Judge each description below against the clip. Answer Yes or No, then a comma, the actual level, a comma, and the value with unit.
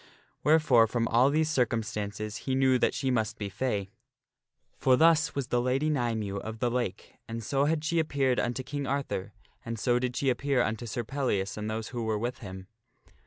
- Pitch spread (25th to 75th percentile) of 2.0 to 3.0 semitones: No, average, 3.7 semitones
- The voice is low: Yes, low, 125 Hz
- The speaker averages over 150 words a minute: Yes, average, 200 wpm